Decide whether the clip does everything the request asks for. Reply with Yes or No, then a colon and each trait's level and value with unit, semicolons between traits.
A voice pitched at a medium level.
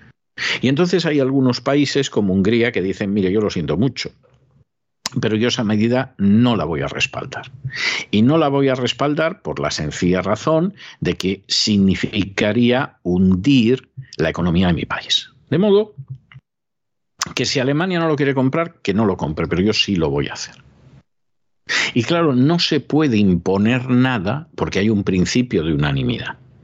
No: low, 125 Hz